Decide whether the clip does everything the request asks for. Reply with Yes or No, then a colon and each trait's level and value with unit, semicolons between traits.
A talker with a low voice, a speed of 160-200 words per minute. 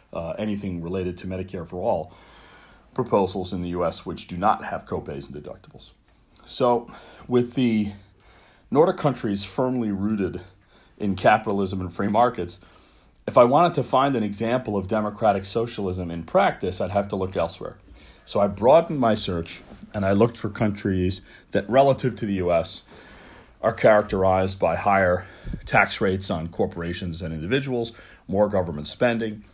No: low, 100 Hz; average, 150 wpm